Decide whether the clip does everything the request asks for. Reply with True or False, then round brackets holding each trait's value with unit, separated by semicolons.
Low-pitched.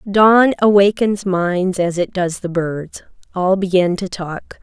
False (185 Hz)